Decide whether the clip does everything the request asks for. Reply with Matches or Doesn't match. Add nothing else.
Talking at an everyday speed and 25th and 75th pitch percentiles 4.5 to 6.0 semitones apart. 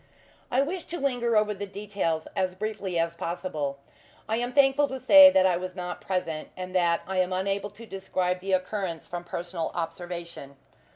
Doesn't match